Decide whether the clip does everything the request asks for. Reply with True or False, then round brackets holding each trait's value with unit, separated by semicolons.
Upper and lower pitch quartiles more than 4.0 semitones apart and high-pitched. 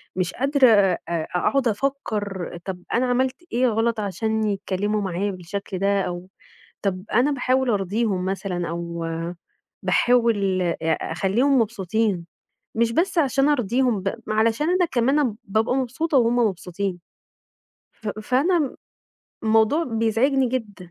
True (4.7 semitones; 220 Hz)